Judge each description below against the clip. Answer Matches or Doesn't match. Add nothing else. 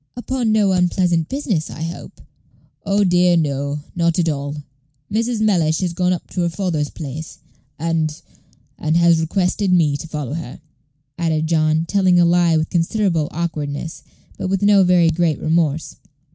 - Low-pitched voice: Doesn't match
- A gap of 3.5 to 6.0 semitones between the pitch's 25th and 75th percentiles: Doesn't match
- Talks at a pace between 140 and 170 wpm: Matches